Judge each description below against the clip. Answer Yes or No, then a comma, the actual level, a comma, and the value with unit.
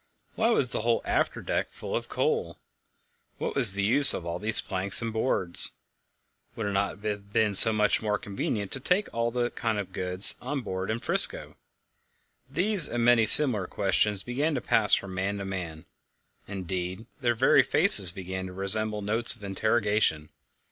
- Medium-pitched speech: No, low, 105 Hz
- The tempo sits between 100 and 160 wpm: No, average, 175 wpm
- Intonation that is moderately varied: Yes, average, 3.6 semitones